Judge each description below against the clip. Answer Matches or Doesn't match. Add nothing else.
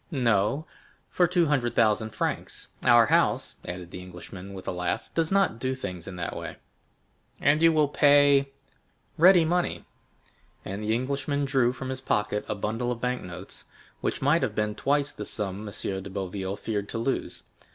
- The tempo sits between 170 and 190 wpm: Matches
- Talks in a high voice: Doesn't match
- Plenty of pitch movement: Matches